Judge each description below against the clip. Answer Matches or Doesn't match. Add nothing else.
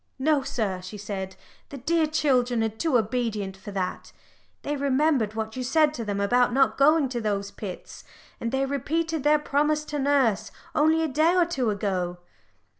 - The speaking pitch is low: Doesn't match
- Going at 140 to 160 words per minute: Doesn't match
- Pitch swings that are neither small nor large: Doesn't match